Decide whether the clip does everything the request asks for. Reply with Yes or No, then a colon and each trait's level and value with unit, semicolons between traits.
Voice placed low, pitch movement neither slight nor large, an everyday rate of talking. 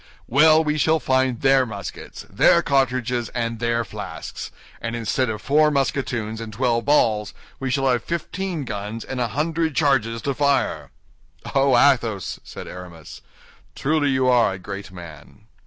Yes: low, 125 Hz; average, 4.0 semitones; average, 155 wpm